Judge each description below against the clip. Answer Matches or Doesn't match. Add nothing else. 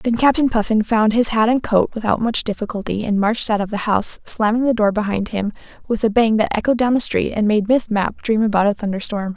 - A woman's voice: Matches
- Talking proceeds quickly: Matches